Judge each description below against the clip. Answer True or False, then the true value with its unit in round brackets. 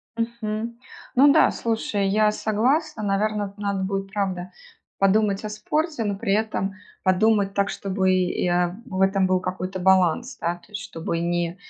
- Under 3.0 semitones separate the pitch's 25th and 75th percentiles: True (2.5 semitones)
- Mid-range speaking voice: False (200 Hz)